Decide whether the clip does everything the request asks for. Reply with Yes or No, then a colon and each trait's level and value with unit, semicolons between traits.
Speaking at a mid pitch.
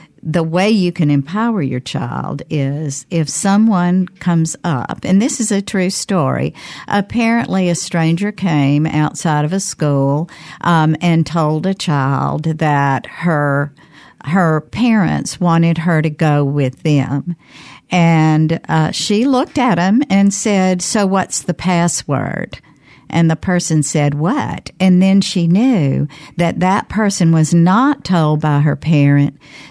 Yes: medium, 165 Hz